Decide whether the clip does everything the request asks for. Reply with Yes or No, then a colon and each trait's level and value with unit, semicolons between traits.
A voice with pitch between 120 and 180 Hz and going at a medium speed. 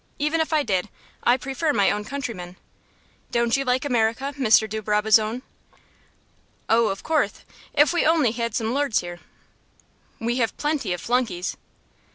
No: high, 235 Hz; average, 155 wpm